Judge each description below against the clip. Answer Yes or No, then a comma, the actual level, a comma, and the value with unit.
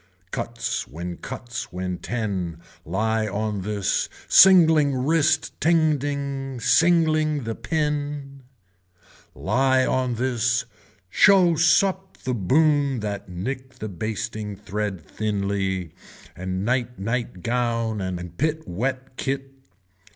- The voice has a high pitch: No, low, 120 Hz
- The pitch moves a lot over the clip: Yes, wide, 5.7 semitones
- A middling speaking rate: No, slow, 105 wpm